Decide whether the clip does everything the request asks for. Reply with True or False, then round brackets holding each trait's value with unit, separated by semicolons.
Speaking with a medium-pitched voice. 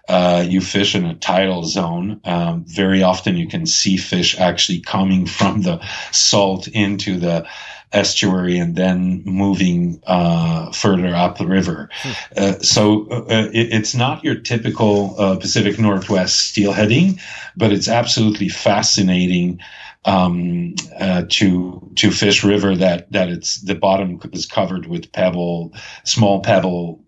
False (95 Hz)